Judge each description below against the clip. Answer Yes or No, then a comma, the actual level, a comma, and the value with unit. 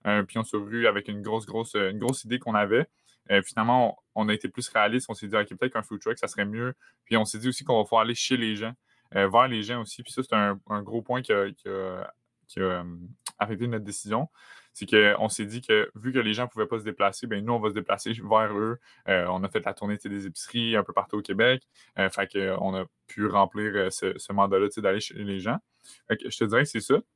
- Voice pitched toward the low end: Yes, low, 110 Hz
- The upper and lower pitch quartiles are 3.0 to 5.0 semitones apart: No, narrow, 2.5 semitones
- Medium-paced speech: No, fast, 265 wpm